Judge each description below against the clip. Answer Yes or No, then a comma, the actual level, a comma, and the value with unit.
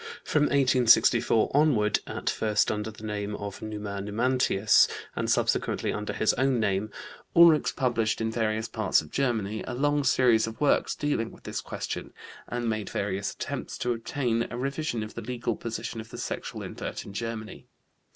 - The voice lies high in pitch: No, low, 115 Hz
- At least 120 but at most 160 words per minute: No, average, 170 wpm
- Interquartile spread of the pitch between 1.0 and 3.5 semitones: Yes, average, 3.0 semitones